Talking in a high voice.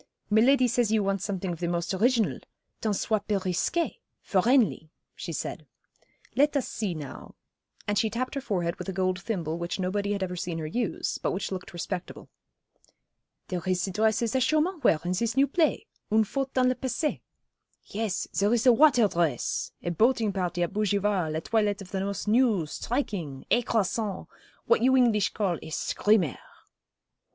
Yes: high, 205 Hz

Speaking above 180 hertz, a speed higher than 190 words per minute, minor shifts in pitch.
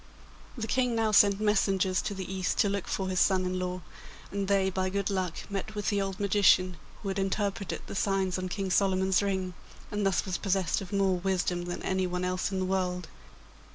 Yes: high, 190 Hz; fast, 205 wpm; narrow, 1.4 semitones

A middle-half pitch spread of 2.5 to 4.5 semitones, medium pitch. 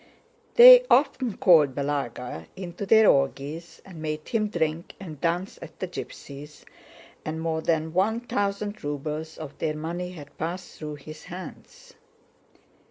Yes: average, 3.9 semitones; medium, 160 Hz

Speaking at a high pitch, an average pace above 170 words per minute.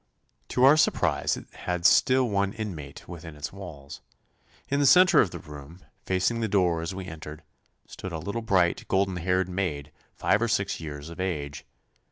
No: very low, 90 Hz; average, 180 wpm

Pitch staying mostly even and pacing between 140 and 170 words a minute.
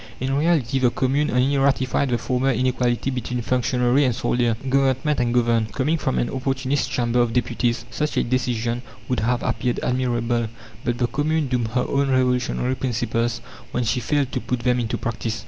No: narrow, 1.9 semitones; average, 180 wpm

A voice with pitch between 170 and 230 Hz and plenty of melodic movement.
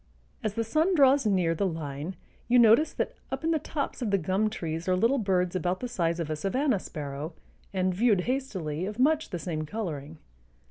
Yes: high, 190 Hz; wide, 6.7 semitones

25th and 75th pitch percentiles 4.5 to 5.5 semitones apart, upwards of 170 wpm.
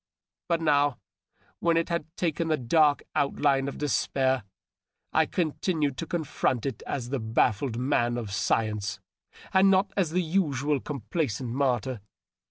No: average, 4.9 semitones; average, 140 wpm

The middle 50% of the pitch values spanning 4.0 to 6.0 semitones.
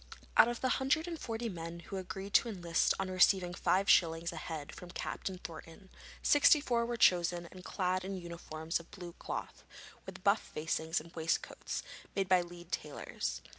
No: average, 2.8 semitones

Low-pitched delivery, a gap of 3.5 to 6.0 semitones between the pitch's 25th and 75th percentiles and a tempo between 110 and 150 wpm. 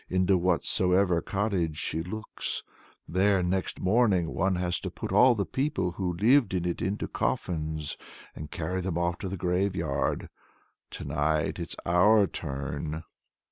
No: very low, 90 Hz; average, 2.9 semitones; average, 145 wpm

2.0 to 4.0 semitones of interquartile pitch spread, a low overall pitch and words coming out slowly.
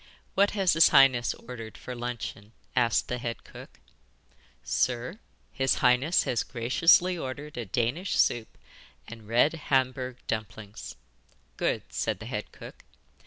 Yes: average, 2.9 semitones; low, 125 Hz; slow, 130 wpm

